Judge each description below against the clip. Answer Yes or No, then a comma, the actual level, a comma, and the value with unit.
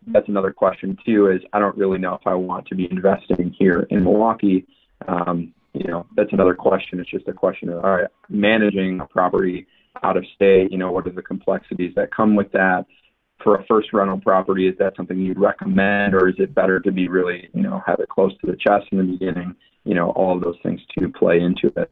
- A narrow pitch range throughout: Yes, narrow, 1.4 semitones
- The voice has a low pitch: Yes, very low, 95 Hz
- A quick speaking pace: Yes, fast, 235 wpm